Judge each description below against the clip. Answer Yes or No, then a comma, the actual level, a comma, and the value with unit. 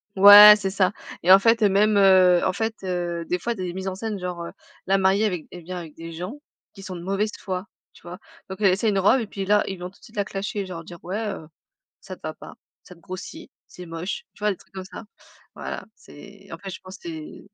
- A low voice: No, high, 190 Hz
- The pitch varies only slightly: Yes, narrow, 2.2 semitones